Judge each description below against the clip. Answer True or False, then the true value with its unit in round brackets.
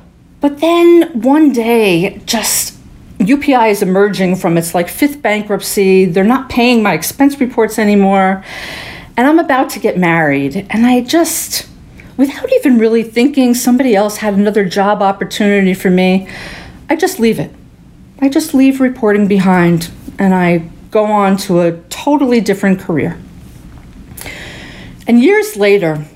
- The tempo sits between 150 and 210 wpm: False (140 wpm)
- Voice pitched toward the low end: False (210 Hz)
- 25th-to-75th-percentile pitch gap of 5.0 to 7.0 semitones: True (5.3 semitones)